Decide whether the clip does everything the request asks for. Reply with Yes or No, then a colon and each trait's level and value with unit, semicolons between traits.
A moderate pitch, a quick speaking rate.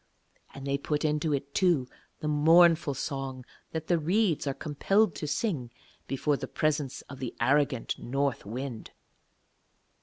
No: medium, 145 Hz; average, 145 wpm